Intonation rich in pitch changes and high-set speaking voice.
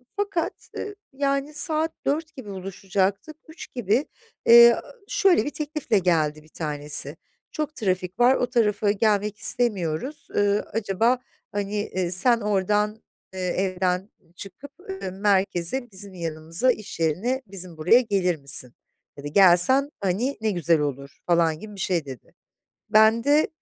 Yes: wide, 5.7 semitones; high, 200 Hz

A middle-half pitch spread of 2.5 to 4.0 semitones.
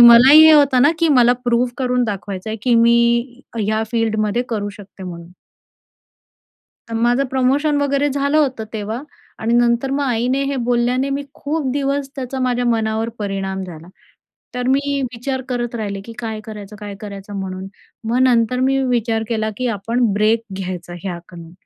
Yes: average, 3.6 semitones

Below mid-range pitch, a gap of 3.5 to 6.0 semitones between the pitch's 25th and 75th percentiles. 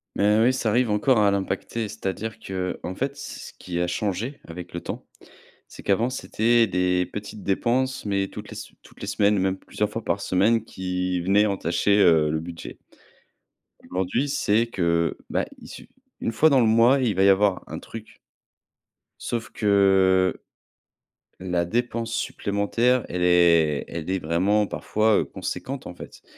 Yes: low, 100 Hz; average, 3.8 semitones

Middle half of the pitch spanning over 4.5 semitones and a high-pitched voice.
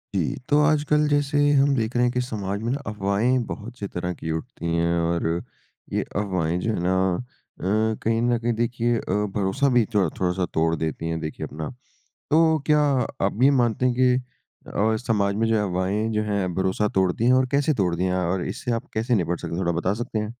No: average, 4.9 semitones; low, 105 Hz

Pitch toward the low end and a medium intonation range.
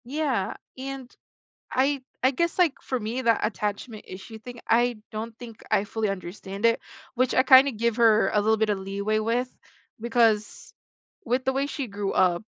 No: high, 230 Hz; average, 3.4 semitones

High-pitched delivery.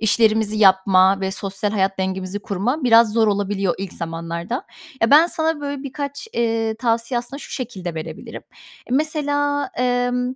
Yes: high, 225 Hz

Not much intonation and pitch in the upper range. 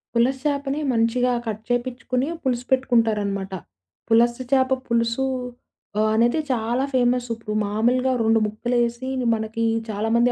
Yes: narrow, 2.0 semitones; high, 235 Hz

